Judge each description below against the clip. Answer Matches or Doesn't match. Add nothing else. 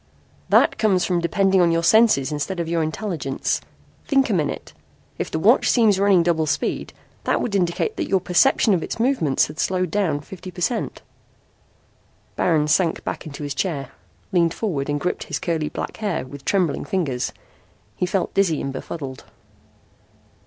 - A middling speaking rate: Matches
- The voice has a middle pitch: Matches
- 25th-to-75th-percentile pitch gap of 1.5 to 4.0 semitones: Doesn't match